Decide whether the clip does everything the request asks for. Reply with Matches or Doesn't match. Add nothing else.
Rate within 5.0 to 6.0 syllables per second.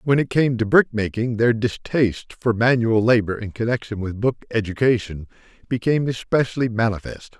Matches